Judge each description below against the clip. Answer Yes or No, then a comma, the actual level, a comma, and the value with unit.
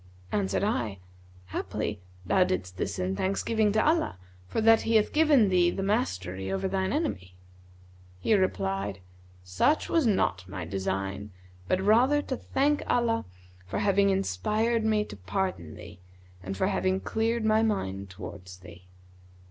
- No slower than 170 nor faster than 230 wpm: No, average, 150 wpm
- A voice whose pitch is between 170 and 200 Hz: Yes, medium, 185 Hz